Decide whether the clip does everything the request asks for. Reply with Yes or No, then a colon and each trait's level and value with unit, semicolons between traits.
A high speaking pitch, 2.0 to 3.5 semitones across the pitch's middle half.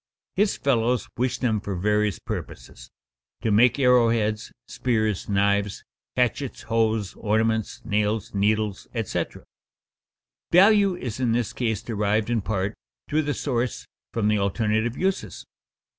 No: low, 110 Hz; average, 2.9 semitones